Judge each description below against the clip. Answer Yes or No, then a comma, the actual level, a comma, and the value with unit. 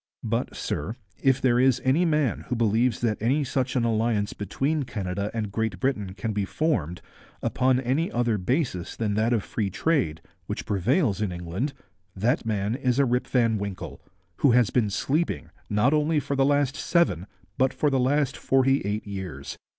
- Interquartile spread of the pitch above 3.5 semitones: Yes, average, 4.7 semitones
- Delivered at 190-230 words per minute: No, average, 180 wpm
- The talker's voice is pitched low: Yes, low, 120 Hz